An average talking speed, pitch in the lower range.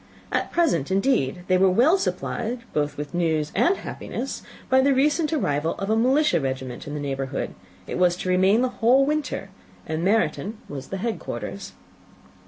No: average, 175 wpm; high, 190 Hz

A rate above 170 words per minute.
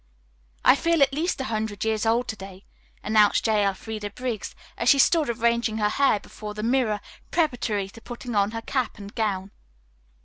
Yes: average, 180 wpm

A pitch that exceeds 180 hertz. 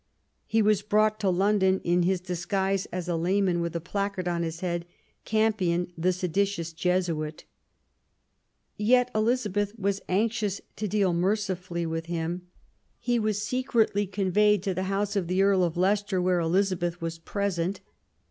Yes: high, 190 Hz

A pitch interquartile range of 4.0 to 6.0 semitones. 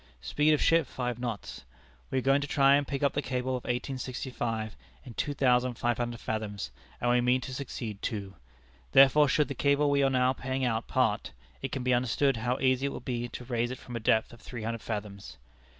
No: narrow, 2.6 semitones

